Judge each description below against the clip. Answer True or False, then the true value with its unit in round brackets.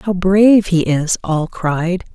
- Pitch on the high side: False (180 Hz)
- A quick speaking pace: False (170 wpm)